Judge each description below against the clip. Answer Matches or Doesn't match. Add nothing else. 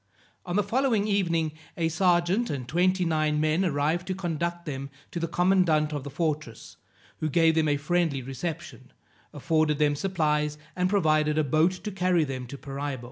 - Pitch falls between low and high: Matches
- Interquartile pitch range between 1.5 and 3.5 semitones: Matches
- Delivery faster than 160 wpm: Matches